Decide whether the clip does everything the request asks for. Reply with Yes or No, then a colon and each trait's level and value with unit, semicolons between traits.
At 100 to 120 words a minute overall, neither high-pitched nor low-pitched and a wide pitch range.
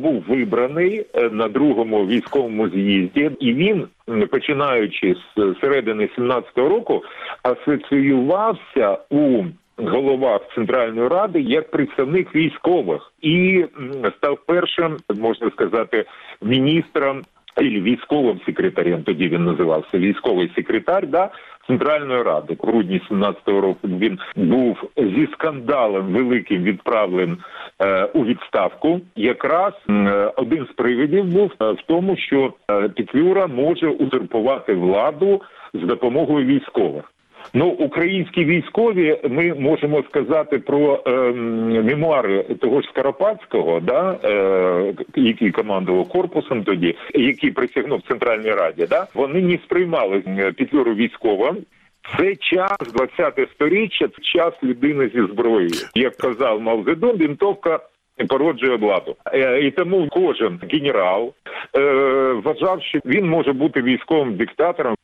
Yes: average, 115 wpm; medium, 155 Hz; wide, 8.3 semitones